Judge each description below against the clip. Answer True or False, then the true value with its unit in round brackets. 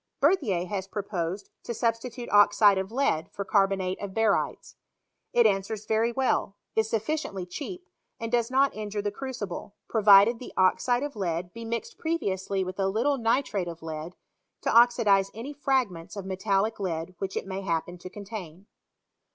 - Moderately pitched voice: False (205 Hz)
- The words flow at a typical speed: True (165 wpm)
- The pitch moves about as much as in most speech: True (3.7 semitones)